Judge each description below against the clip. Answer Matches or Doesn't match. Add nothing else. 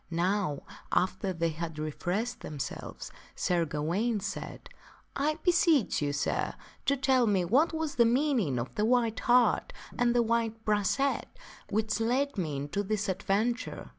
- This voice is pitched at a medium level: Doesn't match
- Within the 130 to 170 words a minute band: Matches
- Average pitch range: Doesn't match